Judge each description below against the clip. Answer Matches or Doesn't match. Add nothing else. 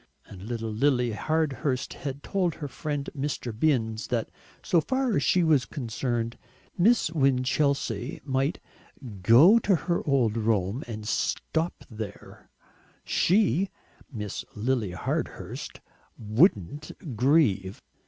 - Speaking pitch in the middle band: Doesn't match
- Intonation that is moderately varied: Doesn't match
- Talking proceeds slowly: Matches